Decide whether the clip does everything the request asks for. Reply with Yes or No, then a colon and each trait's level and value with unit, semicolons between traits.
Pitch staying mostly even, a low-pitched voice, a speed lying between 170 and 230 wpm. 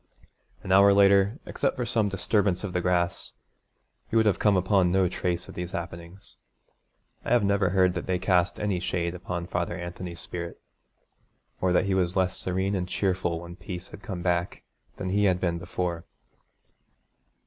Yes: narrow, 2.0 semitones; very low, 90 Hz; average, 175 wpm